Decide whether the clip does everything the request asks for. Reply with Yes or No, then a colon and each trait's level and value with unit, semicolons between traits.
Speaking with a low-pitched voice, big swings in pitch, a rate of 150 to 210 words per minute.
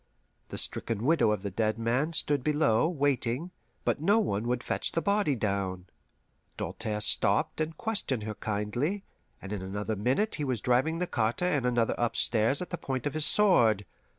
Yes: low, 125 Hz; wide, 6.6 semitones; average, 180 wpm